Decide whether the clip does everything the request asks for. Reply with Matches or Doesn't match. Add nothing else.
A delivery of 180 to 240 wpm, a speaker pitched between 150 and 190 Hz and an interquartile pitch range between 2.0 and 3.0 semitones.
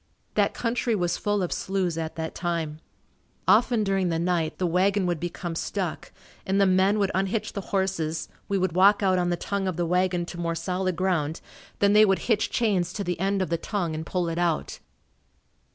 Matches